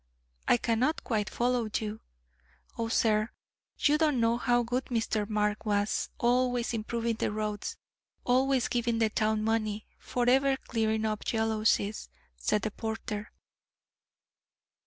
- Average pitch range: No, narrow, 2.2 semitones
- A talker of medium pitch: No, high, 225 Hz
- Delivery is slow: Yes, slow, 125 wpm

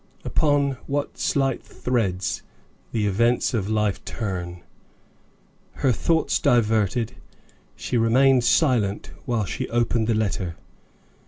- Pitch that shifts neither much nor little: Yes, average, 3.7 semitones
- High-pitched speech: No, low, 115 Hz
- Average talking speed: No, slow, 105 wpm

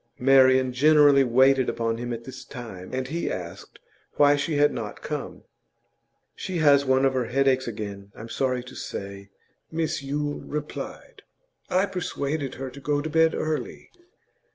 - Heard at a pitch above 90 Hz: Yes, low, 135 Hz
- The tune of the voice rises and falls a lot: No, average, 3.3 semitones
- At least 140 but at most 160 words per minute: Yes, average, 155 wpm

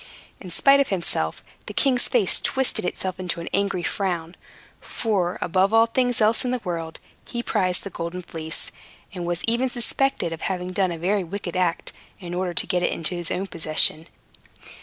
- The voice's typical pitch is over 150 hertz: Yes, medium, 185 Hz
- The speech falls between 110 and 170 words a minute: No, average, 185 wpm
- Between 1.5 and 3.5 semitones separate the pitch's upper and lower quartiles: No, average, 4.2 semitones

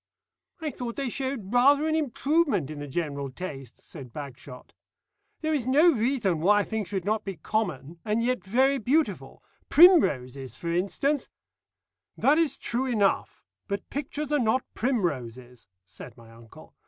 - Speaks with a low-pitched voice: No, high, 215 Hz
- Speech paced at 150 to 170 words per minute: Yes, average, 155 wpm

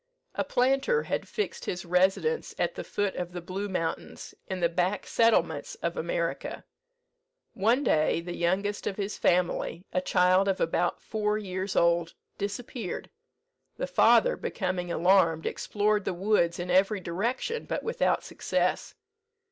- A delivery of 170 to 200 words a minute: No, average, 145 wpm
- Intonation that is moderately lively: Yes, average, 3.3 semitones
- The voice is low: No, high, 190 Hz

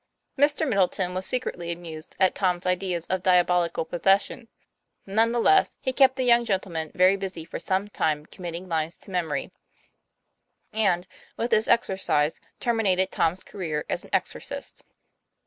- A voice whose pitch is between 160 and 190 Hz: Yes, medium, 185 Hz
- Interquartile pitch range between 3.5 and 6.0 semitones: Yes, average, 4.1 semitones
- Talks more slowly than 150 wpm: No, average, 155 wpm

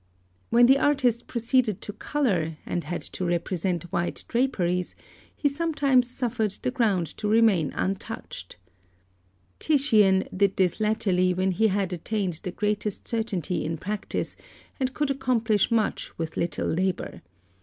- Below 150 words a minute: Yes, slow, 135 wpm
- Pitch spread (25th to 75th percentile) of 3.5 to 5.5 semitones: Yes, average, 5.2 semitones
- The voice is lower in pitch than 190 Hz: No, high, 210 Hz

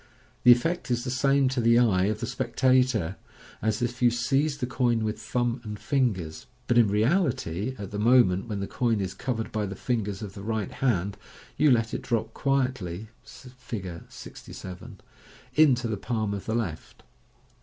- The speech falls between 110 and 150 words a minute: No, average, 180 wpm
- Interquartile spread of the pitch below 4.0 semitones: Yes, average, 3.6 semitones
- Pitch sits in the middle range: No, low, 115 Hz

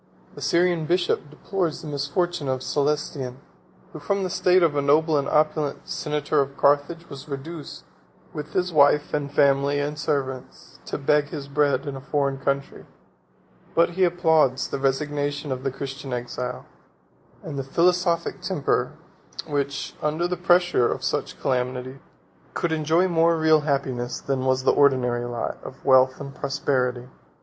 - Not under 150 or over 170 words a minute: Yes, average, 155 wpm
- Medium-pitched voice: Yes, medium, 145 Hz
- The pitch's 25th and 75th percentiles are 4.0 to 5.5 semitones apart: No, average, 2.9 semitones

